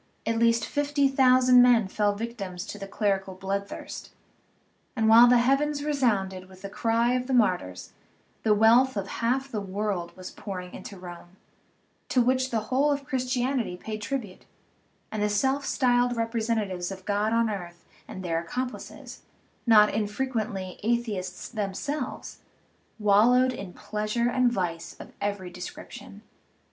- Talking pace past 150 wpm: No, average, 145 wpm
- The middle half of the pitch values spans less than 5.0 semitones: Yes, average, 4.3 semitones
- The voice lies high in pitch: Yes, high, 220 Hz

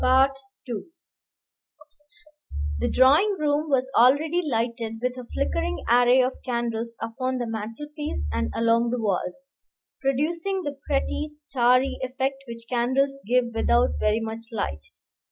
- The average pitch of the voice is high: Yes, very high, 255 Hz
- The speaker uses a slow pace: Yes, slow, 120 wpm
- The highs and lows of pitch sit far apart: No, average, 3.8 semitones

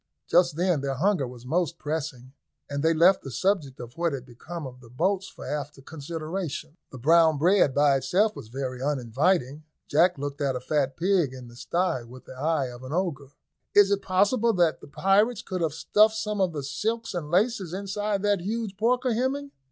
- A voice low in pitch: No, medium, 165 Hz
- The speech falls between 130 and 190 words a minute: No, average, 200 wpm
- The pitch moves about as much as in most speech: No, wide, 6.1 semitones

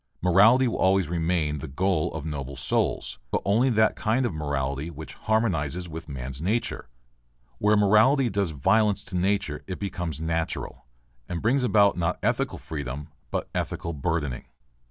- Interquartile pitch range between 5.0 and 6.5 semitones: Yes, wide, 5.6 semitones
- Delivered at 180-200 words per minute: No, average, 155 wpm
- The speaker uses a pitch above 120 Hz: No, very low, 90 Hz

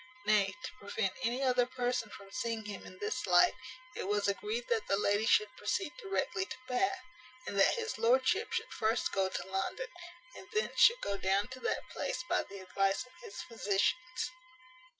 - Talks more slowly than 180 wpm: No, average, 185 wpm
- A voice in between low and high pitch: No, high, 230 Hz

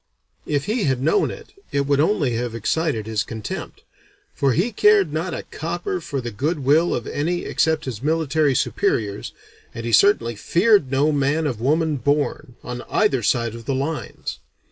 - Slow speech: No, average, 170 wpm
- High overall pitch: No, medium, 145 Hz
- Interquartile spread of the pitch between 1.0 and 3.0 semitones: No, average, 5.0 semitones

